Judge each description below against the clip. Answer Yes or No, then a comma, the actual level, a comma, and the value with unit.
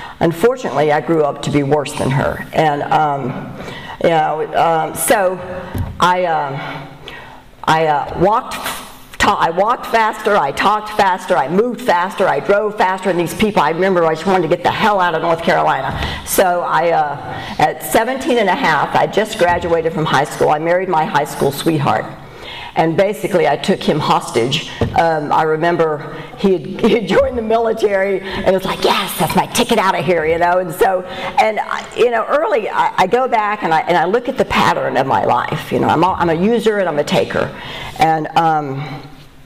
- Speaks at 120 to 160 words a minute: No, average, 200 wpm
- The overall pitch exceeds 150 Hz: Yes, medium, 185 Hz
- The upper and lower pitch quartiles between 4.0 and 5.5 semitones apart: Yes, average, 4.5 semitones